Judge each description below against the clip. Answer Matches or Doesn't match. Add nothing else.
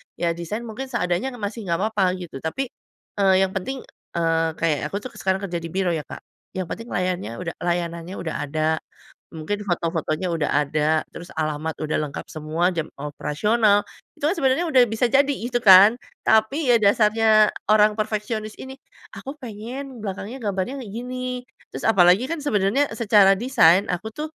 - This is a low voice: Doesn't match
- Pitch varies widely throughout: Matches